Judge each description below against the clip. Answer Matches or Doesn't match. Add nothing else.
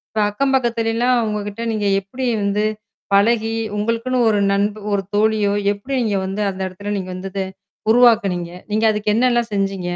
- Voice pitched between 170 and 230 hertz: Matches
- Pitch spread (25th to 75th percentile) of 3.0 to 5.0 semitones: Doesn't match